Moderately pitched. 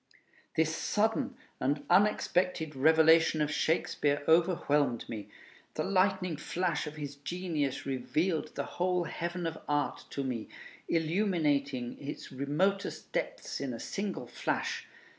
Yes: medium, 160 Hz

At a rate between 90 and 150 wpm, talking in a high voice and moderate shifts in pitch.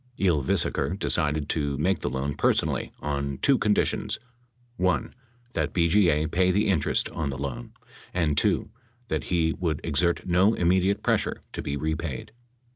No: average, 145 wpm; very low, 80 Hz; average, 4.1 semitones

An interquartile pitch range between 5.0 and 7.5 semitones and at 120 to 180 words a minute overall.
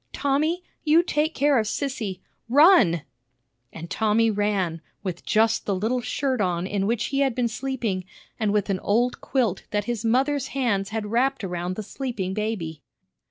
Yes: average, 5.3 semitones; average, 165 wpm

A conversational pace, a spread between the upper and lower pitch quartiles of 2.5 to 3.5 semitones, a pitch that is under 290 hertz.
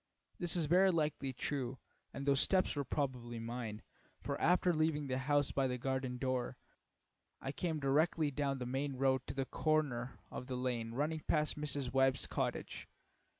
Yes: average, 170 wpm; average, 3.0 semitones; low, 135 Hz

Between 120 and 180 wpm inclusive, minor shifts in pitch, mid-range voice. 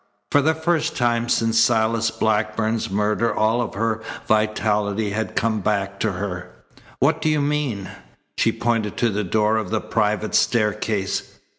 No: average, 155 wpm; narrow, 1.7 semitones; low, 110 Hz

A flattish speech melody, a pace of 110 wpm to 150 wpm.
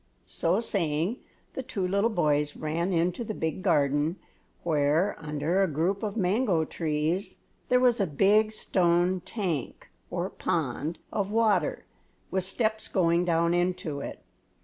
No: average, 4.1 semitones; average, 140 wpm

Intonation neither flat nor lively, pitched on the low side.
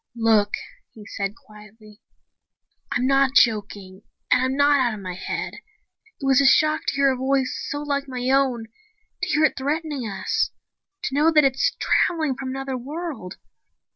No: average, 4.3 semitones; very high, 265 Hz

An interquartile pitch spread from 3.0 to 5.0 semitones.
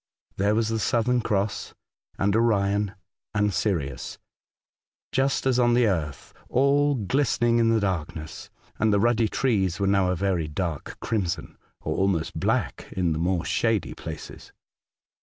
Yes: average, 4.2 semitones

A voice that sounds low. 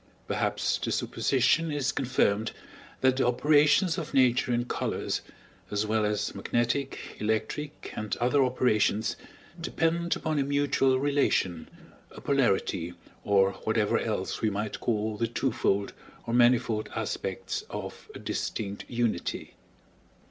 Yes: low, 120 Hz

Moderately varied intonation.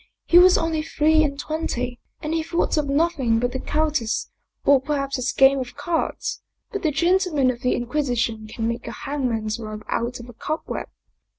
Yes: average, 4.4 semitones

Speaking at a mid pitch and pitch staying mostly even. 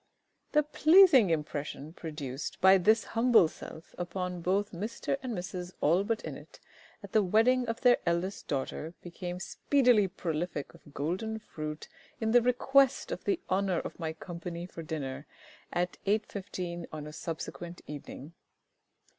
No: medium, 180 Hz; average, 5.3 semitones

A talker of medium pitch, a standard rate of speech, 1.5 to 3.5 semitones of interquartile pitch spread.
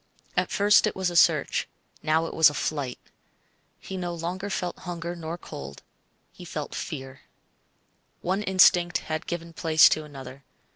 Yes: medium, 170 Hz; average, 155 wpm; narrow, 2.4 semitones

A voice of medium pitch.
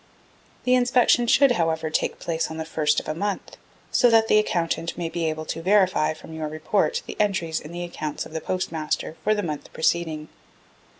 Yes: medium, 165 Hz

